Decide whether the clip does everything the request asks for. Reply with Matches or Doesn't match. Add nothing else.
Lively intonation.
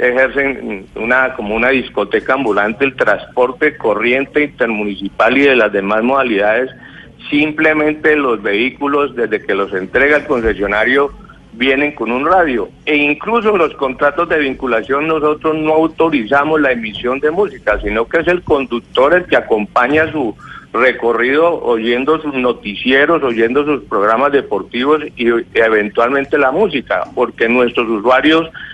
Doesn't match